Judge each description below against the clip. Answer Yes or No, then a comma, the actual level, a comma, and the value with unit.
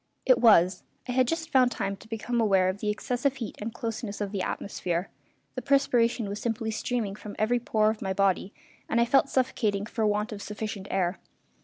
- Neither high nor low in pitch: No, high, 215 Hz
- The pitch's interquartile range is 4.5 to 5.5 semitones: No, average, 3.3 semitones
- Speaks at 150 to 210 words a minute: Yes, average, 200 wpm